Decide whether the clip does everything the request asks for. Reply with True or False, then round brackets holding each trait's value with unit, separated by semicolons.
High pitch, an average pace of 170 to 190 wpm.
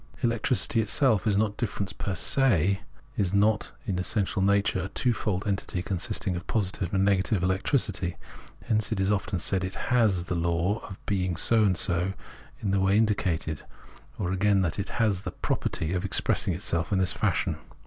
False (95 Hz; 180 wpm)